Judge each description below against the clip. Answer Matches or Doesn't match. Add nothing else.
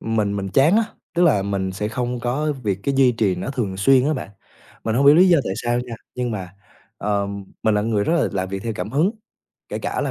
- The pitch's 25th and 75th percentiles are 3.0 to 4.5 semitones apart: Doesn't match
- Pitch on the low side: Matches